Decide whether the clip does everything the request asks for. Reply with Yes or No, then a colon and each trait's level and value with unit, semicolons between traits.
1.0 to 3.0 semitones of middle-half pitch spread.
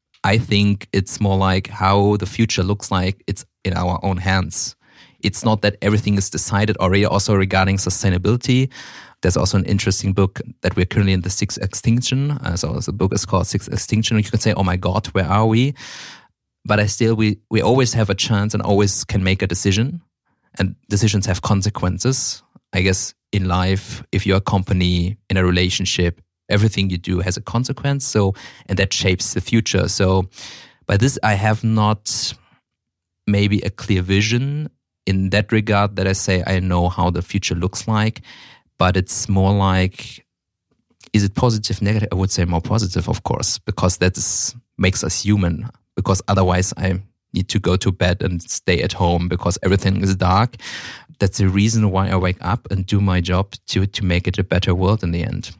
Yes: narrow, 2.5 semitones